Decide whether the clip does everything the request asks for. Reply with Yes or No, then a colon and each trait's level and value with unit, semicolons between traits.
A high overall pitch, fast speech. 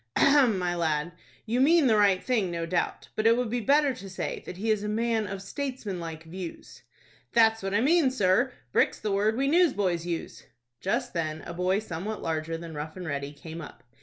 Yes: high, 195 Hz; fast, 210 wpm